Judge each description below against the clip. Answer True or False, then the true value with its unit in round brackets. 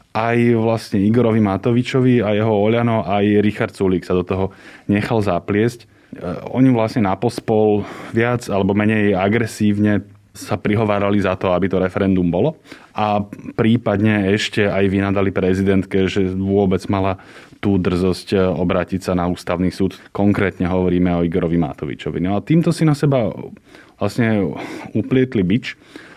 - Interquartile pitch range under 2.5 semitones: False (2.8 semitones)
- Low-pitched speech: True (100 Hz)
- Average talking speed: True (140 wpm)